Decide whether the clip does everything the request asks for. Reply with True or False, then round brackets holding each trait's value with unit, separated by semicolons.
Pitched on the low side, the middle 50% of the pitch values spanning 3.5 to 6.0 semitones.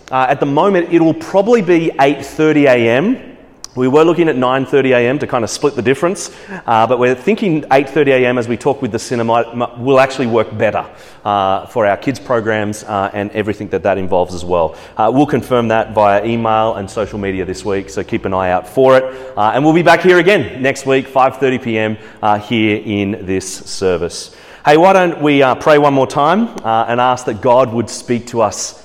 True (125 Hz; 5.1 semitones)